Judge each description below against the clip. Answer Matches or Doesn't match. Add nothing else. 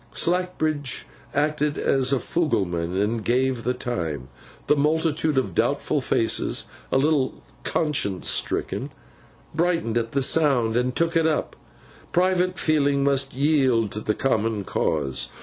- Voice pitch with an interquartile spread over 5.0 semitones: Matches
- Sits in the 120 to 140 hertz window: Matches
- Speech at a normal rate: Doesn't match